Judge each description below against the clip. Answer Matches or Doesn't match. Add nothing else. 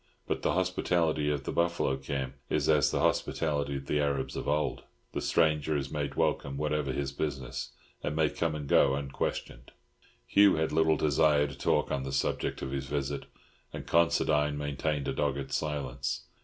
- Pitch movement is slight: Matches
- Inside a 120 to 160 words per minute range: Doesn't match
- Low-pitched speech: Matches